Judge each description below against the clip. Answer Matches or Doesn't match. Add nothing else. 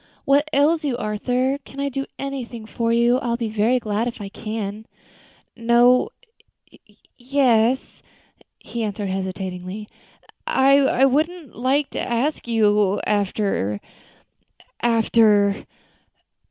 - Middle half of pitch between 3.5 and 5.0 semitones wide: Matches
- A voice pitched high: Matches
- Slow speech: Matches